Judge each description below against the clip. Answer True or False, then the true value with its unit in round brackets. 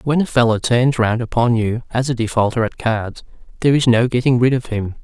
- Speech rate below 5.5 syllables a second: False (5.9 syllables/s)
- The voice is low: True (120 Hz)